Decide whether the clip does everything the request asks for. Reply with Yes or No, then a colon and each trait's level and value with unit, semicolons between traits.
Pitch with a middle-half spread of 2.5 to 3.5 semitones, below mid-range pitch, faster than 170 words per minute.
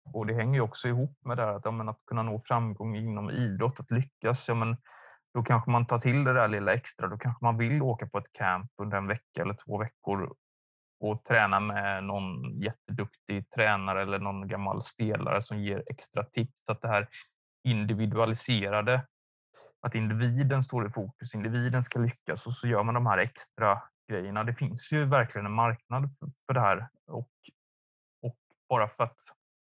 Yes: average, 3.0 semitones; low, 115 Hz; average, 185 wpm